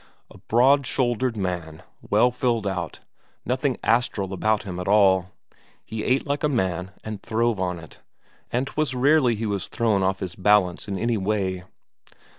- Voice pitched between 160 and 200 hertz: No, low, 105 Hz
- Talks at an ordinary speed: Yes, average, 165 wpm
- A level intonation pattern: No, average, 4.5 semitones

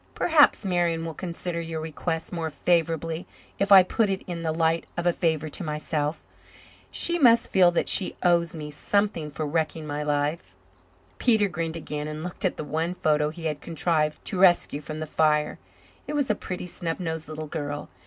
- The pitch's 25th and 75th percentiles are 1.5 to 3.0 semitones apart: Yes, narrow, 2.6 semitones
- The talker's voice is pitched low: No, medium, 165 Hz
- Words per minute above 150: Yes, average, 190 wpm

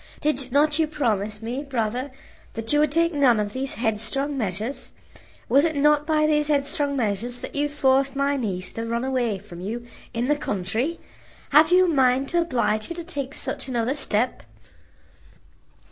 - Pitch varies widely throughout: No, average, 4.6 semitones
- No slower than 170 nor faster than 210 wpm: Yes, average, 175 wpm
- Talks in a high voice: Yes, very high, 265 Hz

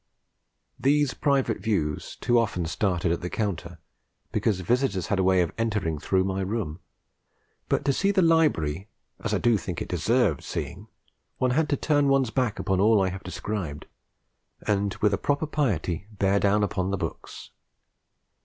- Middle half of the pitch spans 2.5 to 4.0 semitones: No, average, 5.3 semitones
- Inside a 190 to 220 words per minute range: No, average, 170 wpm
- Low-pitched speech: Yes, low, 100 Hz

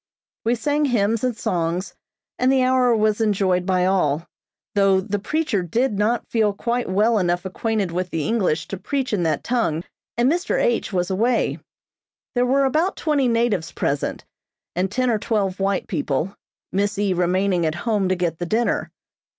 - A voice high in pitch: Yes, high, 205 Hz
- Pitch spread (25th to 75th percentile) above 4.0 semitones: Yes, average, 4.7 semitones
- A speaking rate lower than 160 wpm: No, average, 175 wpm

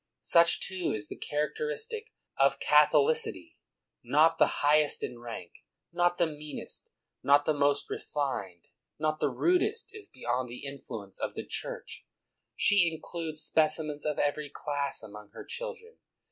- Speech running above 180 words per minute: No, average, 145 wpm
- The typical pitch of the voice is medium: Yes, medium, 150 Hz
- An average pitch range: Yes, average, 3.8 semitones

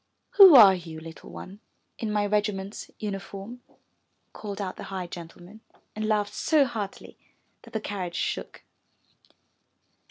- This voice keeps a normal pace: No, slow, 130 wpm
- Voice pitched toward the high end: Yes, high, 205 Hz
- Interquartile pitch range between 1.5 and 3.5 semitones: Yes, narrow, 2.4 semitones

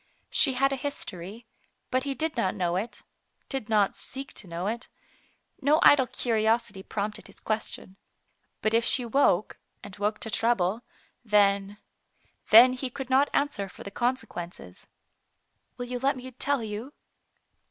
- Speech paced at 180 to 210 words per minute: No, average, 165 wpm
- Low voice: No, high, 230 Hz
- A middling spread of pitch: Yes, average, 4.2 semitones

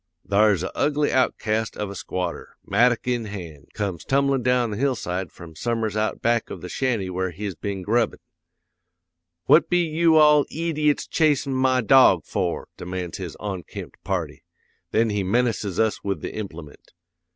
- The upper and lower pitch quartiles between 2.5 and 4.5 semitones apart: No, wide, 5.4 semitones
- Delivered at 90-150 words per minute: No, average, 160 wpm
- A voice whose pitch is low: Yes, low, 110 Hz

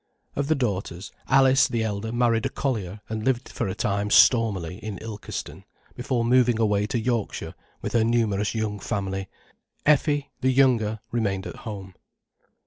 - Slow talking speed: No, average, 155 wpm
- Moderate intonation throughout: Yes, average, 3.3 semitones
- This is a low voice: Yes, low, 110 Hz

